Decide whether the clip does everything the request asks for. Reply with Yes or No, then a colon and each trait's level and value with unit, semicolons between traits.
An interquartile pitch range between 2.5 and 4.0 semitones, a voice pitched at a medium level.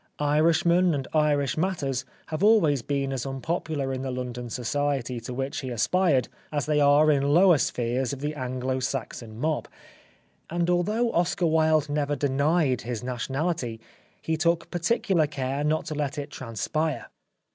Yes: average, 3.6 semitones; medium, 145 Hz